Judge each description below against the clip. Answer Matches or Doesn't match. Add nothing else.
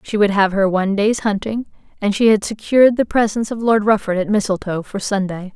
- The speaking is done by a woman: Matches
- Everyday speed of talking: Doesn't match